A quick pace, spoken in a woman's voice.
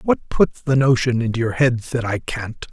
No: fast, 220 wpm; male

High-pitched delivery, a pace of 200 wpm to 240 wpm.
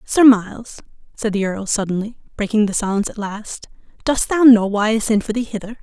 Yes: high, 215 Hz; fast, 205 wpm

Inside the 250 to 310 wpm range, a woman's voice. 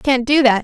Yes: fast, 285 wpm; female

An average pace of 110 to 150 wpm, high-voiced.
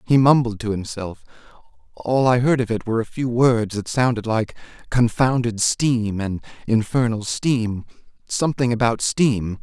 No: average, 145 wpm; low, 115 Hz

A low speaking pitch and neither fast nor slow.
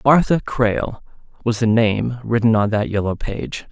Yes: low, 115 Hz; average, 160 wpm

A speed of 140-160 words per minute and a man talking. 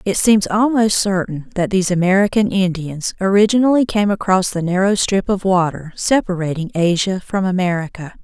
No: average, 145 wpm; female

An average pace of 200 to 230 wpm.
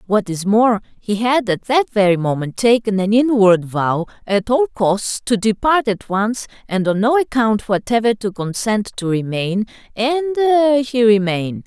No: average, 165 wpm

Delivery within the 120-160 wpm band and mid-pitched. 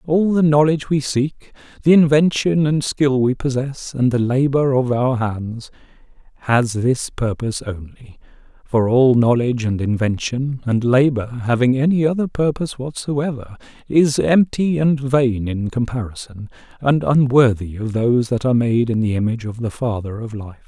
No: average, 155 wpm; low, 125 Hz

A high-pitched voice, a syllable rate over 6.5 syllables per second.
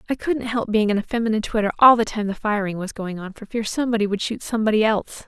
Yes: high, 215 Hz; 7.0 syllables/s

